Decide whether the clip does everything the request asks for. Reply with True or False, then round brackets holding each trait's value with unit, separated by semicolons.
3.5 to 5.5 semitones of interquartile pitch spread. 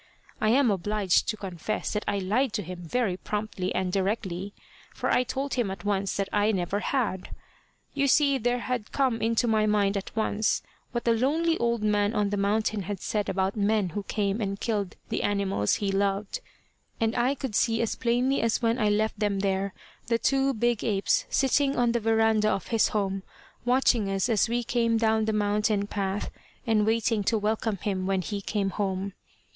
False (2.7 semitones)